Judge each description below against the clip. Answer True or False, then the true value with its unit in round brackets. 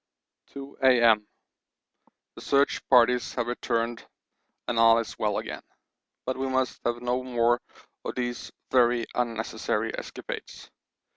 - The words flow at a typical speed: False (125 wpm)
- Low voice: True (120 Hz)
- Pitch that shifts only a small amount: True (1.7 semitones)